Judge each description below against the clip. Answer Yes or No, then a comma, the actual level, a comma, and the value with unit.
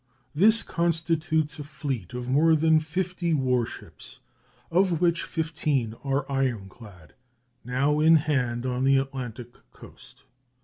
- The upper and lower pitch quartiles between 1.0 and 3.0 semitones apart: No, average, 4.4 semitones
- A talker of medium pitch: Yes, medium, 145 Hz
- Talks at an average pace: No, slow, 125 wpm